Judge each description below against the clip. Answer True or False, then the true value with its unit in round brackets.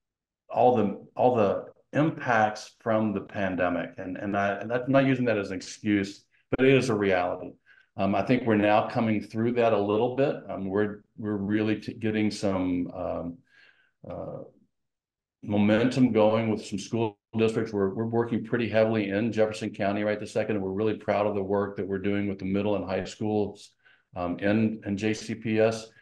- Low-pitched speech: True (105 Hz)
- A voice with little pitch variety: True (1.9 semitones)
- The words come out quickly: False (190 wpm)